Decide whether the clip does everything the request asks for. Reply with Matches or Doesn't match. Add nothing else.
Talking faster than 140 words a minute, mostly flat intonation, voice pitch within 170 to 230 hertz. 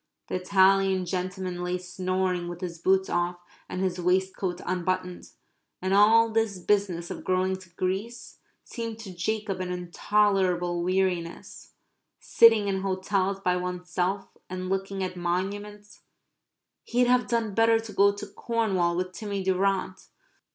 Doesn't match